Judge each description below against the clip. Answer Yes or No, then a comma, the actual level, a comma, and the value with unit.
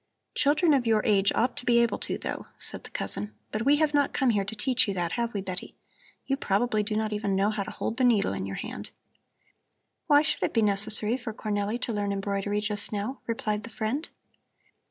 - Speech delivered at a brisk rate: Yes, fast, 220 wpm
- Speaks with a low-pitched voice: No, high, 215 Hz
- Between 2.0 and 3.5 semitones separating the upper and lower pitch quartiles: Yes, average, 3.1 semitones